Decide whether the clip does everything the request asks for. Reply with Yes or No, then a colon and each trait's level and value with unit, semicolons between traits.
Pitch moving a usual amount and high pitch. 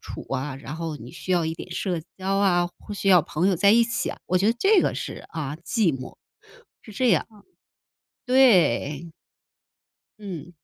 No: average, 4.5 semitones; medium, 180 Hz